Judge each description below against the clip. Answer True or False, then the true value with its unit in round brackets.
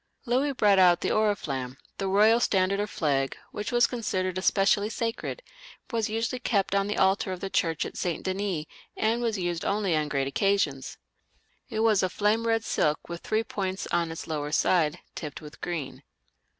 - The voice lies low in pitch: False (195 Hz)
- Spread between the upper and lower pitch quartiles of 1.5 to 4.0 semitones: False (4.7 semitones)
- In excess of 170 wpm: True (180 wpm)